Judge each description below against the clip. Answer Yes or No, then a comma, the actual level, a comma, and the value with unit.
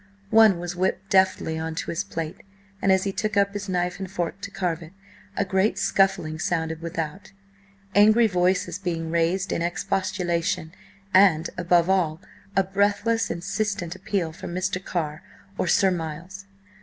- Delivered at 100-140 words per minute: No, average, 155 wpm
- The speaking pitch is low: No, medium, 185 Hz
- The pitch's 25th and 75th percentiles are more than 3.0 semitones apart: No, average, 2.7 semitones